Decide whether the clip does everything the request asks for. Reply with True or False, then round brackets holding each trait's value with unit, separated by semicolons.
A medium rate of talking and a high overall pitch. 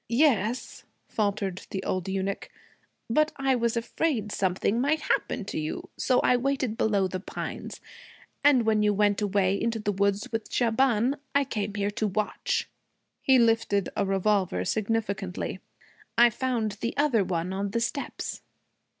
True (150 wpm; 215 Hz)